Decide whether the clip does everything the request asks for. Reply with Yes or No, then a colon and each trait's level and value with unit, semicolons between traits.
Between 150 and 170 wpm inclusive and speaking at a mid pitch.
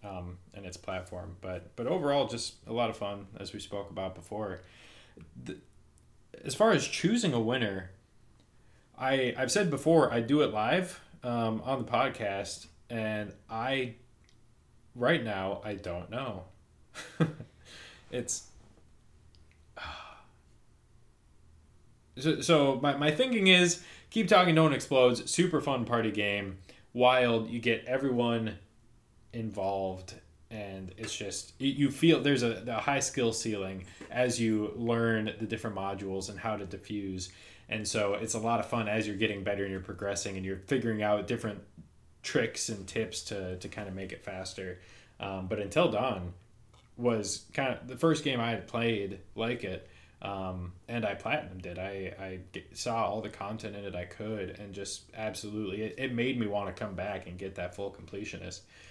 No: average, 165 wpm; low, 105 Hz